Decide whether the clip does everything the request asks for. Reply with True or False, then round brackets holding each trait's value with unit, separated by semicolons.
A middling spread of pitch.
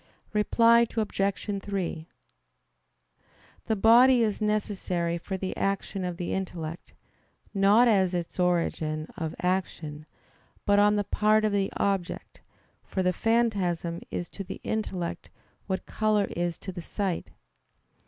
True (3.3 semitones)